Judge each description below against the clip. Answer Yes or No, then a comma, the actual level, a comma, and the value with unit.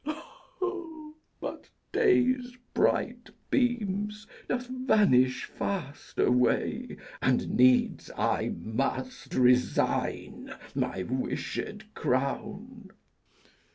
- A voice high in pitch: Yes, high, 205 Hz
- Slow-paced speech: Yes, slow, 70 wpm